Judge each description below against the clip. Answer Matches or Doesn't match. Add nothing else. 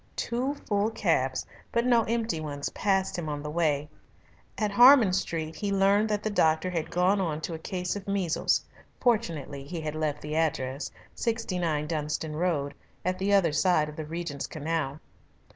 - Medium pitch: Matches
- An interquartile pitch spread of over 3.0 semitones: Matches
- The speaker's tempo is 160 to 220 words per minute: Matches